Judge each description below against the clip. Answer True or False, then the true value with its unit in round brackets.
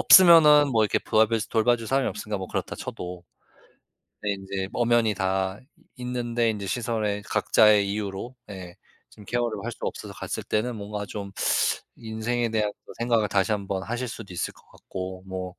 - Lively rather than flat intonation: False (3.3 semitones)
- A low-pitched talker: True (105 Hz)